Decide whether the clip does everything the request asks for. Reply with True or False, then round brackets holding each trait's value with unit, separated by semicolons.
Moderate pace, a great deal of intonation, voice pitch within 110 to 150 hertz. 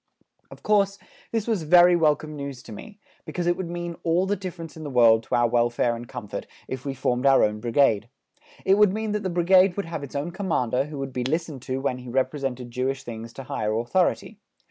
False (220 wpm; 6.2 semitones; 140 Hz)